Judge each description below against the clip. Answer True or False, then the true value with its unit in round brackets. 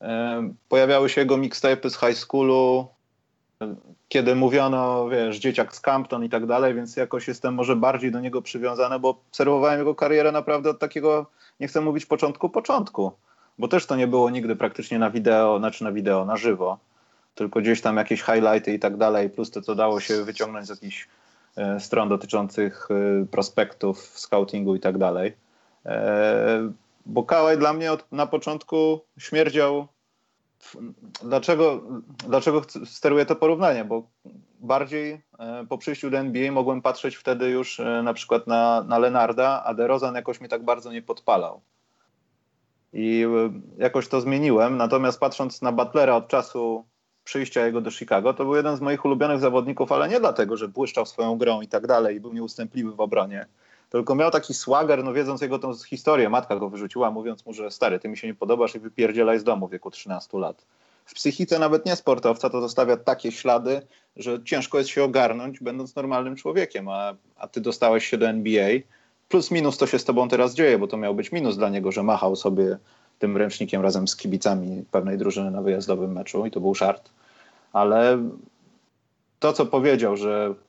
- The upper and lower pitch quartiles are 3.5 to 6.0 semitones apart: True (3.8 semitones)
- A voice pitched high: False (125 Hz)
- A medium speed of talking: False (175 wpm)